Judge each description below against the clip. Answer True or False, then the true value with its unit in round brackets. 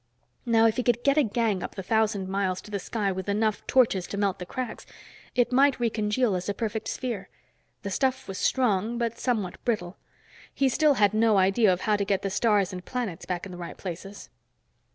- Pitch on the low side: False (210 Hz)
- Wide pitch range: False (3.6 semitones)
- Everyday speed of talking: False (215 wpm)